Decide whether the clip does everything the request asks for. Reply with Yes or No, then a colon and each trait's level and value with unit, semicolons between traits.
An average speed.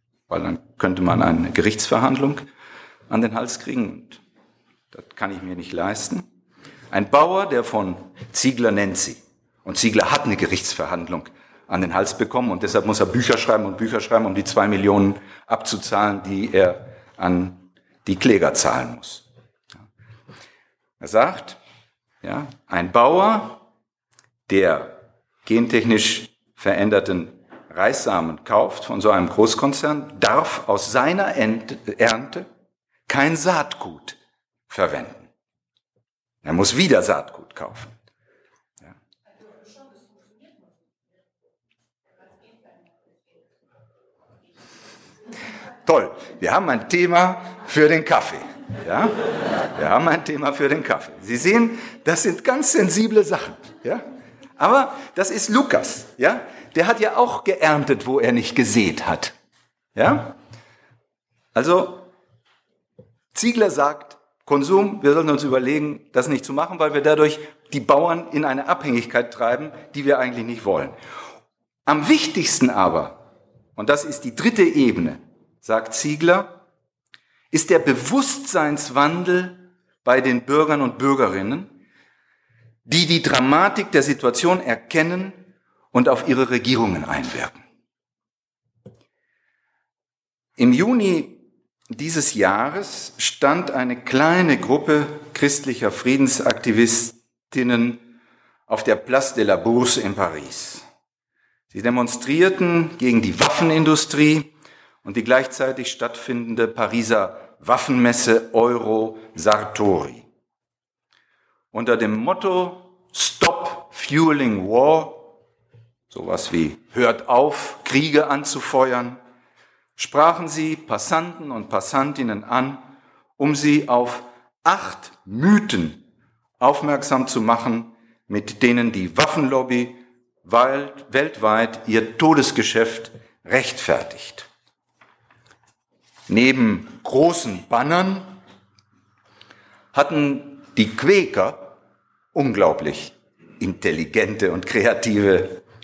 No: slow, 105 wpm